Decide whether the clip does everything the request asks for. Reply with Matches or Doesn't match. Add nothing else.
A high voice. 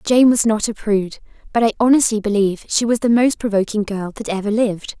Matches